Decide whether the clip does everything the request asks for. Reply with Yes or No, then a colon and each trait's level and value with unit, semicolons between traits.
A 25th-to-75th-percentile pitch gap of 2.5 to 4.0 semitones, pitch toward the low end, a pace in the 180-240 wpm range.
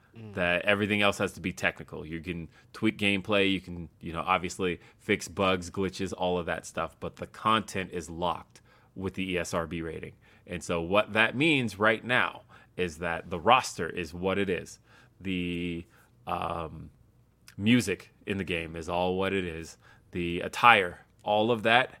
No: average, 3.4 semitones; very low, 95 Hz; average, 170 wpm